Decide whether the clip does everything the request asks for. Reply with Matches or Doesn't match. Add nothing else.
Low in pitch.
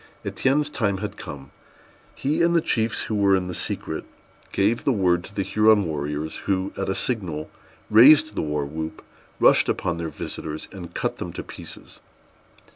Matches